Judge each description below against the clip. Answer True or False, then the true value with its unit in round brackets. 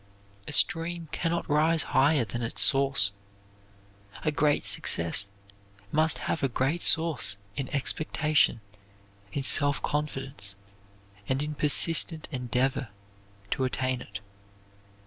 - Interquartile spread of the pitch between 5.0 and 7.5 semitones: False (3.2 semitones)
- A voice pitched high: False (140 Hz)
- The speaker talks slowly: True (115 wpm)